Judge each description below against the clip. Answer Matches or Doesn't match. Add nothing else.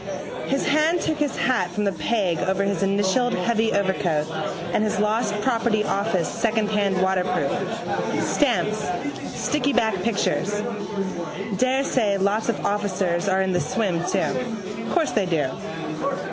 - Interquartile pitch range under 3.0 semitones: Doesn't match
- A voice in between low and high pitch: Doesn't match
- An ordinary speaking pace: Doesn't match